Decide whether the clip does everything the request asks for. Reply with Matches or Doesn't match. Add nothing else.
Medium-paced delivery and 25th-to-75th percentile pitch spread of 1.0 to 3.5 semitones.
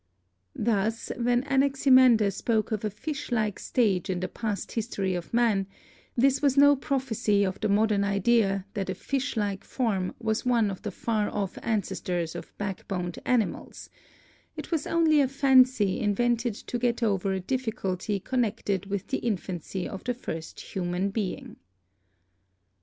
Doesn't match